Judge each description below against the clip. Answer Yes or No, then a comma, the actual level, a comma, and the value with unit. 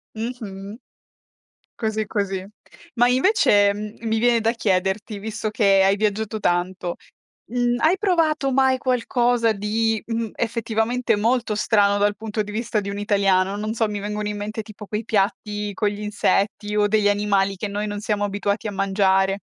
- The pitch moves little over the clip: Yes, narrow, 2.0 semitones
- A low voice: No, high, 210 Hz